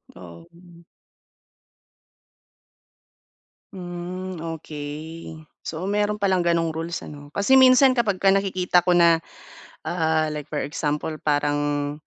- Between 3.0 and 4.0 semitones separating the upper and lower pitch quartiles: Yes, average, 3.7 semitones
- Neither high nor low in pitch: Yes, medium, 170 Hz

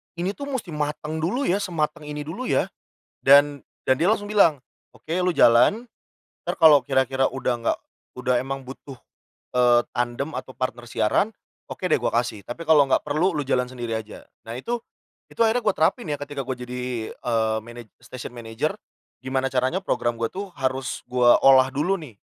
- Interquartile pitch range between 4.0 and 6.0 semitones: Yes, average, 5.0 semitones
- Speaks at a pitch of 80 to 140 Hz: Yes, low, 135 Hz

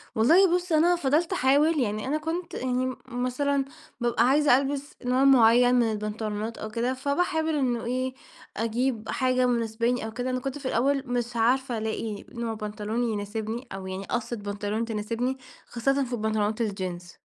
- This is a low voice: No, high, 245 Hz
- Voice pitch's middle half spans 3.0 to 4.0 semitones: Yes, average, 3.6 semitones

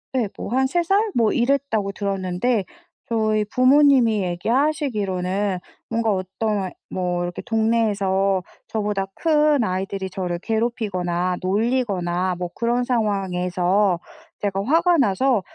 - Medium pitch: No, high, 210 Hz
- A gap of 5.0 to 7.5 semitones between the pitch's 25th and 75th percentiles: No, average, 4.5 semitones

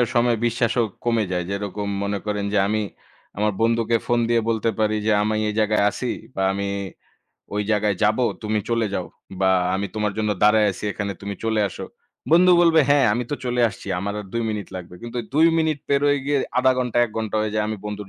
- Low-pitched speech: Yes, low, 110 Hz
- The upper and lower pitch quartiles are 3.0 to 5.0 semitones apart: No, narrow, 2.5 semitones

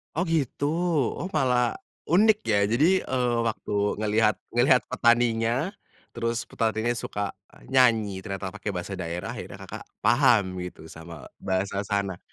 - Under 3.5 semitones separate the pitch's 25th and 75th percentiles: No, average, 4.2 semitones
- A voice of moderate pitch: No, low, 115 Hz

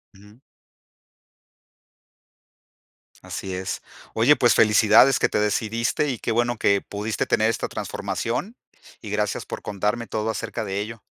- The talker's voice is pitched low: Yes, low, 110 Hz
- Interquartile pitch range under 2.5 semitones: Yes, narrow, 2.1 semitones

